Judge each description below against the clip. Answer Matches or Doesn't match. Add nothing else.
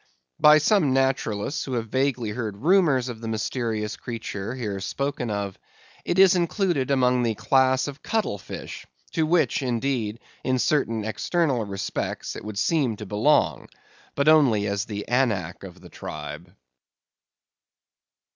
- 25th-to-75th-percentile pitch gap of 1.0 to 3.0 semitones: Doesn't match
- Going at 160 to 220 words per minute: Doesn't match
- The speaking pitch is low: Matches